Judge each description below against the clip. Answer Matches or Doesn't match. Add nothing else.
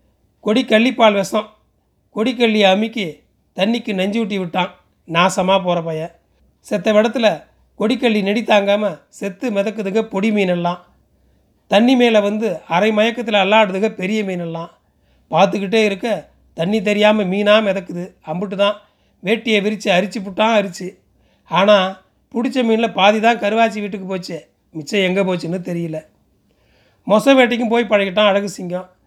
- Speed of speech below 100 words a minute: Doesn't match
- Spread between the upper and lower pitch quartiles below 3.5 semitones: Matches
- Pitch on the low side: Doesn't match